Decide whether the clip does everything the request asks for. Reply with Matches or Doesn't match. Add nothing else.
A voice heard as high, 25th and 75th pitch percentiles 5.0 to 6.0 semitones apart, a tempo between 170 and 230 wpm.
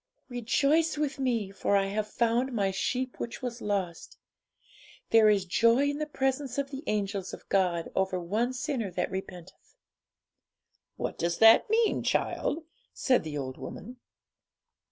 Doesn't match